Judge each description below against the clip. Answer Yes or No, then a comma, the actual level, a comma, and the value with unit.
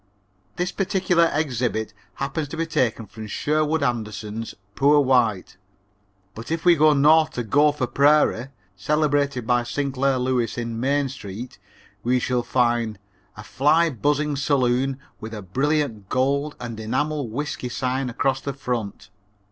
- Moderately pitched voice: No, low, 130 Hz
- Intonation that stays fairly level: No, average, 3.9 semitones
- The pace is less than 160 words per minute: Yes, average, 140 wpm